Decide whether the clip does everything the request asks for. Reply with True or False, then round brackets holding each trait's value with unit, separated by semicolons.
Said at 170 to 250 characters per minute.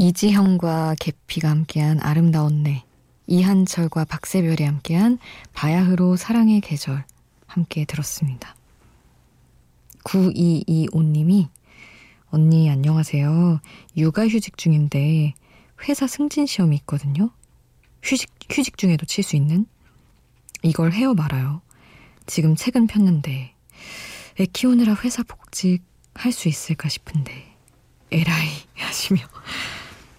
True (235 characters per minute)